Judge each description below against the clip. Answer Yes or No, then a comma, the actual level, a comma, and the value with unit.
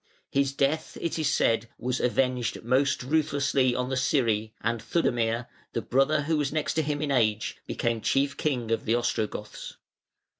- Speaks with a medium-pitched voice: No, low, 130 Hz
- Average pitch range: Yes, average, 3.5 semitones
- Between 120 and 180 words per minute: Yes, average, 160 wpm